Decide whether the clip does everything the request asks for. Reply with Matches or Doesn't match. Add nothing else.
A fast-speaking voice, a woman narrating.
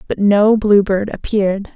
Doesn't match